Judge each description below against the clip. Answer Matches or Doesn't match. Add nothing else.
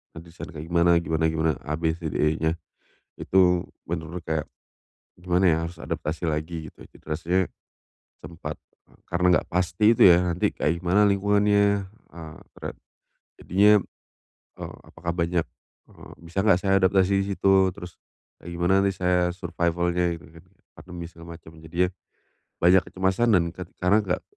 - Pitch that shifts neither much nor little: Doesn't match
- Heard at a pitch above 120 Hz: Doesn't match